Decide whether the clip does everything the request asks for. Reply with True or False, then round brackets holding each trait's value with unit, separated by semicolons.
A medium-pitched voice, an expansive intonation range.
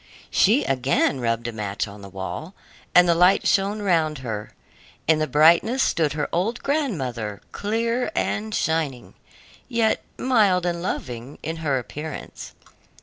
True (160 Hz; 8.4 semitones)